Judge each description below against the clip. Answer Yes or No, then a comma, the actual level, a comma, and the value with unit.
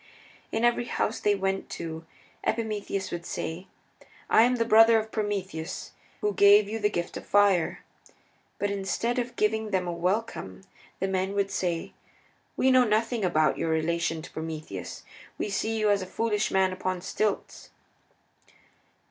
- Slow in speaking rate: No, average, 155 wpm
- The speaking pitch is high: Yes, high, 200 Hz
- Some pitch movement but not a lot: Yes, average, 3.4 semitones